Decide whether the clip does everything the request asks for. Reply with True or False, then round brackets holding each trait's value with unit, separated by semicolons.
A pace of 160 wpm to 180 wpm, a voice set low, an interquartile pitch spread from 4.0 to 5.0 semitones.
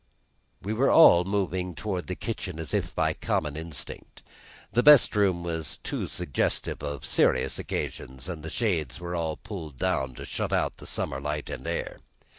True (175 wpm; 85 Hz; 4.3 semitones)